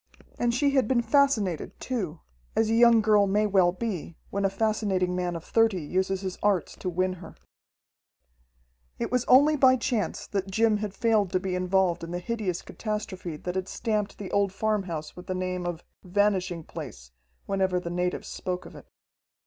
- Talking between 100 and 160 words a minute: No, average, 180 wpm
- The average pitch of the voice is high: Yes, high, 195 Hz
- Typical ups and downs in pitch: Yes, average, 3.4 semitones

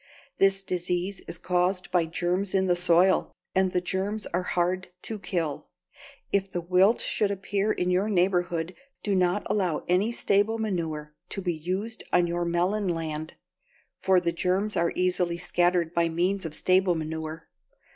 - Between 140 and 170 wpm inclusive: Yes, average, 160 wpm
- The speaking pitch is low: No, medium, 180 Hz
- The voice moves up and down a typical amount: No, narrow, 2.1 semitones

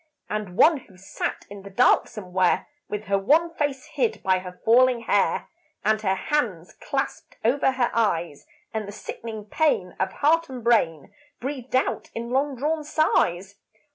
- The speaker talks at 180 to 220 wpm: No, average, 165 wpm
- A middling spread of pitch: No, wide, 5.9 semitones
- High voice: Yes, high, 225 Hz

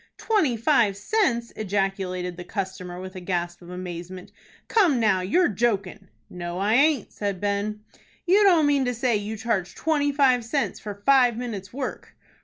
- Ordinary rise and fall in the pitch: No, wide, 6.0 semitones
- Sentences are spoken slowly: No, average, 165 wpm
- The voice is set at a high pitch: Yes, high, 210 Hz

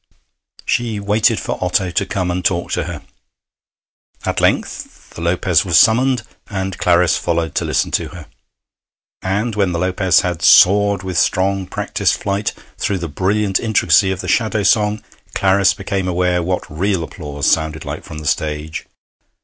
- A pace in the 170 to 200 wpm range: No, average, 160 wpm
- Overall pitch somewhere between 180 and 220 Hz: No, very low, 95 Hz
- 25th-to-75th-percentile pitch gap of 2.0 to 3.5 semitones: Yes, average, 2.7 semitones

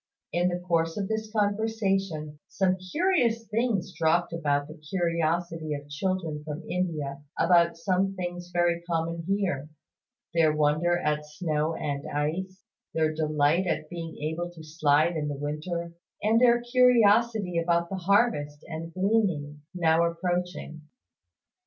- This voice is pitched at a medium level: Yes, medium, 170 Hz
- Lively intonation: No, average, 3.6 semitones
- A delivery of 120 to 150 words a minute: Yes, slow, 135 wpm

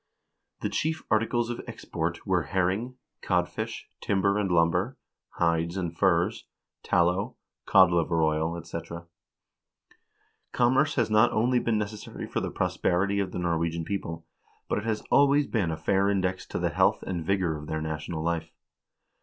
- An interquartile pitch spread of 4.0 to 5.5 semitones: Yes, average, 4.4 semitones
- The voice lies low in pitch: Yes, very low, 95 Hz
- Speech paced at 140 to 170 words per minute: Yes, average, 155 wpm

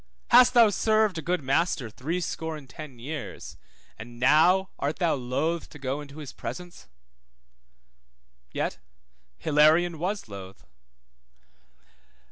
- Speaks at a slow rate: Yes, slow, 115 wpm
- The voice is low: No, medium, 155 Hz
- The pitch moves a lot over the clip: No, average, 4.8 semitones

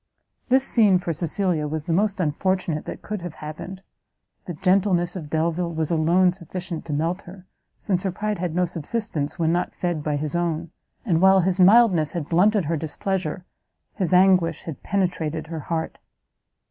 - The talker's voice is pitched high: No, medium, 175 Hz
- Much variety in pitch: No, average, 2.9 semitones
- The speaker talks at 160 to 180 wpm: Yes, average, 170 wpm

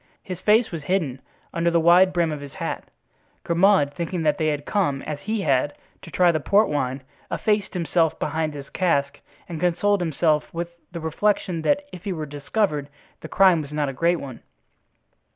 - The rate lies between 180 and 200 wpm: Yes, average, 190 wpm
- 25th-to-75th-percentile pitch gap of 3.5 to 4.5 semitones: Yes, average, 3.9 semitones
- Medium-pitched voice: Yes, medium, 165 Hz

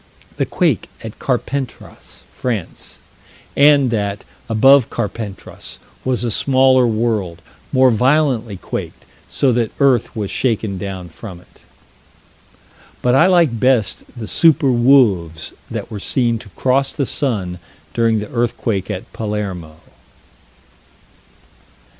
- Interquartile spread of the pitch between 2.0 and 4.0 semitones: No, average, 4.4 semitones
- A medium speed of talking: No, slow, 115 wpm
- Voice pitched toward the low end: Yes, low, 115 Hz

